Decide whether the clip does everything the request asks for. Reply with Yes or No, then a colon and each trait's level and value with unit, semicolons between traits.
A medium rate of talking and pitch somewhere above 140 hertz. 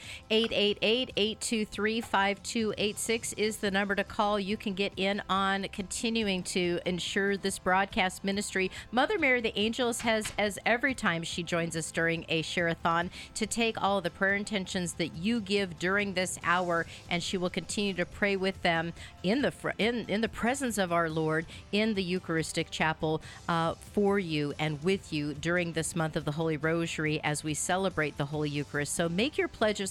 Yes: average, 185 wpm; high, 190 Hz